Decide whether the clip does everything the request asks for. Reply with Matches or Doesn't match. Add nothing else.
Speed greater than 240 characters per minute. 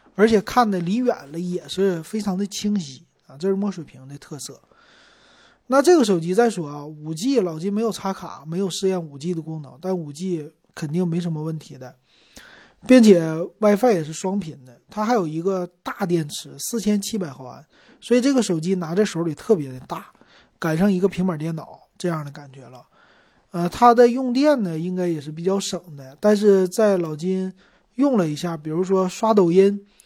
Matches